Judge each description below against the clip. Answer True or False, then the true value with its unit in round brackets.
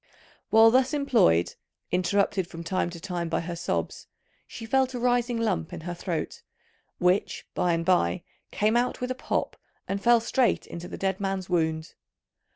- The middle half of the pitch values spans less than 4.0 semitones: False (5.6 semitones)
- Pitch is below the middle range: False (190 Hz)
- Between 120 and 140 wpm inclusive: False (170 wpm)